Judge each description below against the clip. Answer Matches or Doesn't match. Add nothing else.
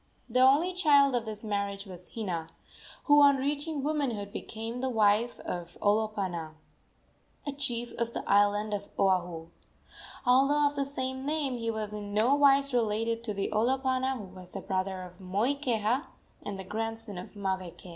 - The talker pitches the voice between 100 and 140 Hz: Doesn't match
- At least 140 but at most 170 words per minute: Matches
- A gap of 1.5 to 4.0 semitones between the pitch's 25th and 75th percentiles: Doesn't match